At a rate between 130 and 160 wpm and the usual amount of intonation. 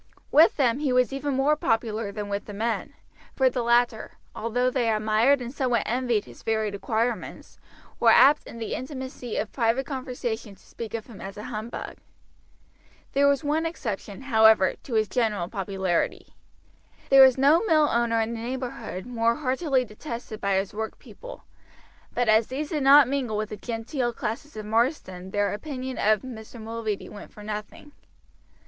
No: average, 170 wpm; average, 3.5 semitones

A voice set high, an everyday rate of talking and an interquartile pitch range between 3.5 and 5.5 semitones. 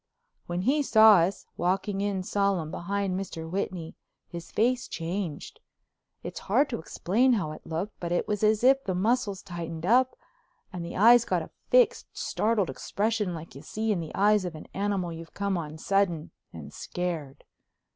Yes: high, 195 Hz; average, 175 wpm; average, 3.8 semitones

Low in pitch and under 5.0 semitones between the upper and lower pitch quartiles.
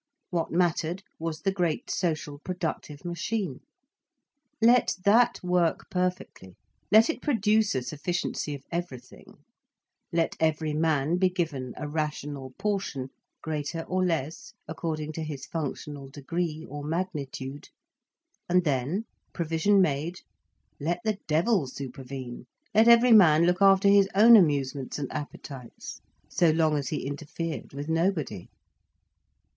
No: medium, 160 Hz; average, 4.1 semitones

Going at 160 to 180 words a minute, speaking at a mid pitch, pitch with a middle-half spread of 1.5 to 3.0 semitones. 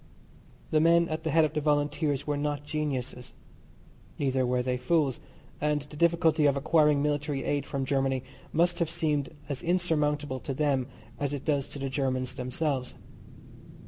Yes: average, 165 wpm; medium, 145 Hz; narrow, 2.4 semitones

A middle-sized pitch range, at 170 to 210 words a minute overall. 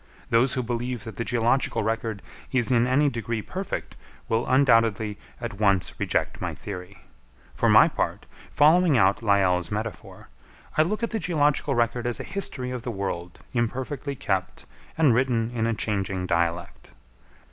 No: average, 4.1 semitones; average, 160 wpm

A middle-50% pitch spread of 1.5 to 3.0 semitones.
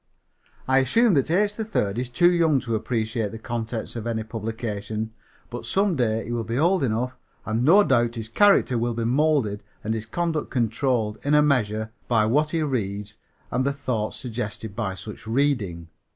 No: average, 4.3 semitones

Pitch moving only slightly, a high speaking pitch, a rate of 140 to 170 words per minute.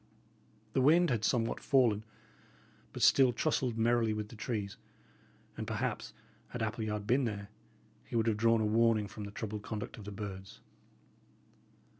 No: narrow, 2.2 semitones; low, 110 Hz; average, 155 wpm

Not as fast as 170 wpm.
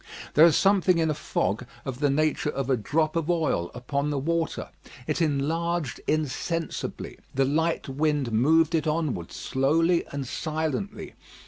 Yes: average, 150 wpm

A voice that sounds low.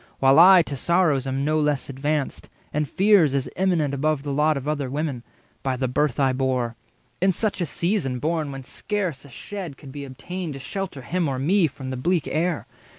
No: medium, 150 Hz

